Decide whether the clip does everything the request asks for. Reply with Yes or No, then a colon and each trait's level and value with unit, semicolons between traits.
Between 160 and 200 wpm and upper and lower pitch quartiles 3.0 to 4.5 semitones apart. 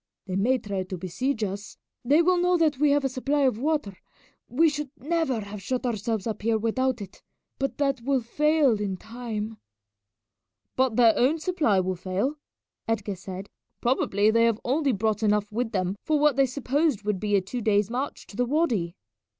No: average, 190 wpm; average, 5.3 semitones